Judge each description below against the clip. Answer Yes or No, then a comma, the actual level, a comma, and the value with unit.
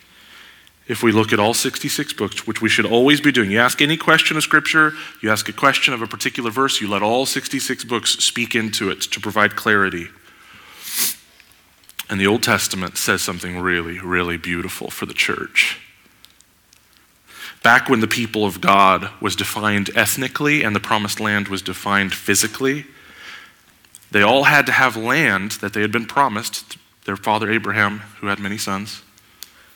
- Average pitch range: Yes, average, 4.4 semitones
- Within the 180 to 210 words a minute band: No, average, 170 wpm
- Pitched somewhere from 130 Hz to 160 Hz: No, low, 110 Hz